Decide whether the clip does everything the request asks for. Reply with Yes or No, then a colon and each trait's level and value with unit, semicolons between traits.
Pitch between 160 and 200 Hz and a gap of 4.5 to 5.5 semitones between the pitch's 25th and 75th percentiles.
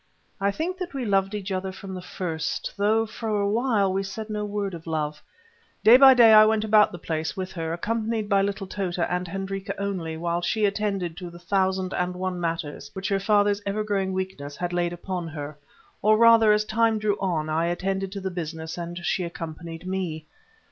No: high, 190 Hz; average, 3.4 semitones